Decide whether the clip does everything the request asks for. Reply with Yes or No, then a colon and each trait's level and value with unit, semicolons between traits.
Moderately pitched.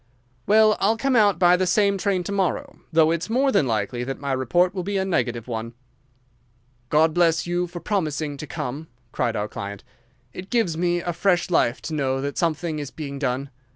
Yes: medium, 165 Hz